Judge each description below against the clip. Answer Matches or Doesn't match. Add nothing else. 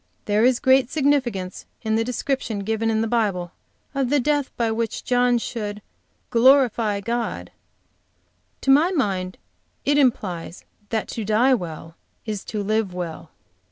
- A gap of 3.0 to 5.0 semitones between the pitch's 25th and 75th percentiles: Matches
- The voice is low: Doesn't match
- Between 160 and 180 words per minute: Doesn't match